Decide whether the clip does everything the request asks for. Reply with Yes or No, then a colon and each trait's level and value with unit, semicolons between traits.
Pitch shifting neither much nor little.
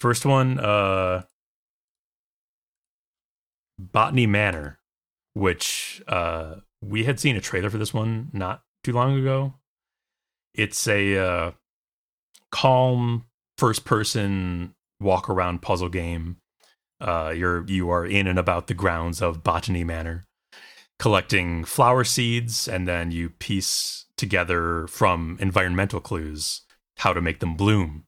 Yes: average, 4.3 semitones